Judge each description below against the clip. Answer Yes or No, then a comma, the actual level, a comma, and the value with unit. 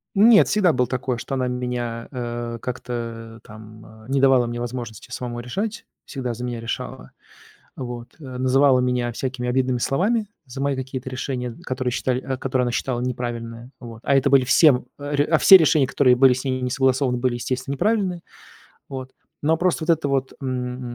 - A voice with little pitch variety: Yes, narrow, 2.1 semitones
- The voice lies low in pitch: Yes, low, 125 Hz